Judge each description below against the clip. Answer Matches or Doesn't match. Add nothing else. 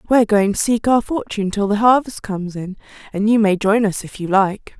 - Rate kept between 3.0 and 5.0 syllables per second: Doesn't match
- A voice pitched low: Doesn't match